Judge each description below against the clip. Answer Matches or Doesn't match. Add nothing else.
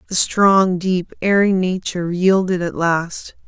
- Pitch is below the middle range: Doesn't match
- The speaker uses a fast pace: Doesn't match